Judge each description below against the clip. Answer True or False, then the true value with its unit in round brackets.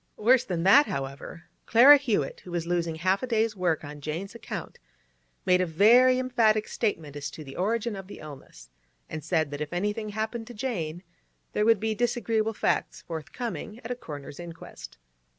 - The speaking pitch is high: True (195 Hz)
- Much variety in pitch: True (6.2 semitones)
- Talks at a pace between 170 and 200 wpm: True (180 wpm)